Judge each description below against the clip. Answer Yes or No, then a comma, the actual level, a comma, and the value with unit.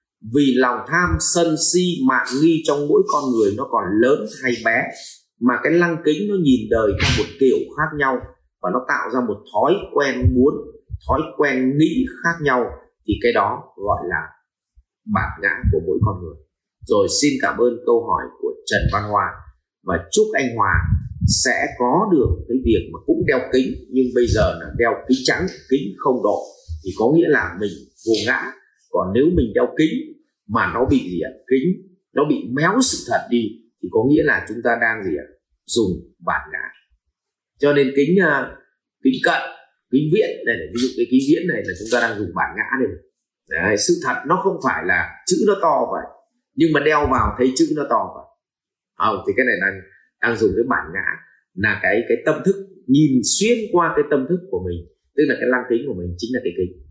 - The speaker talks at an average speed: Yes, average, 210 wpm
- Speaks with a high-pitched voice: No, medium, 170 Hz